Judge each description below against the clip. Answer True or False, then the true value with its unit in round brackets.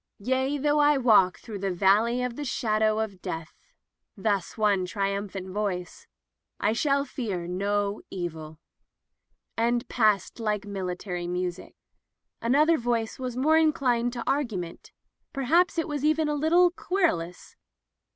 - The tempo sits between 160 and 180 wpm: False (150 wpm)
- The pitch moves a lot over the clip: True (6.2 semitones)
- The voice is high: True (220 Hz)